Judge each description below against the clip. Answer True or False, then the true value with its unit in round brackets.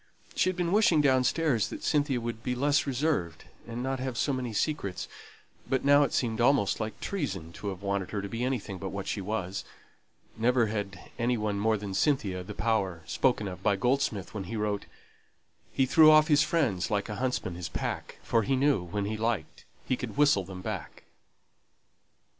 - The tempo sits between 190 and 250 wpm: True (195 wpm)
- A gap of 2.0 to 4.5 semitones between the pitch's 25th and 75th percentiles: False (5.1 semitones)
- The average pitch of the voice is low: True (115 Hz)